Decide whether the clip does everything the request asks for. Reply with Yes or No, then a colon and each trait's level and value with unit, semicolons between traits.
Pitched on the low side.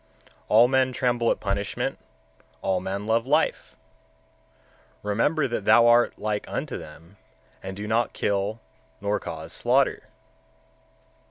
Yes: low, 110 Hz